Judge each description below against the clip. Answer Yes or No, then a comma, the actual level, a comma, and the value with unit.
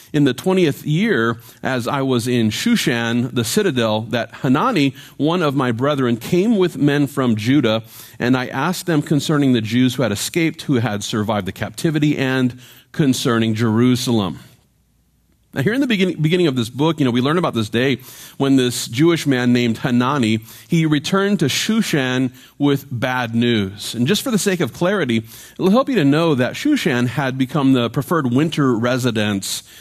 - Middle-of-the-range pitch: No, low, 130 Hz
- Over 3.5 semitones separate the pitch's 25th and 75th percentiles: Yes, average, 4.6 semitones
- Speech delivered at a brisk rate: No, average, 180 wpm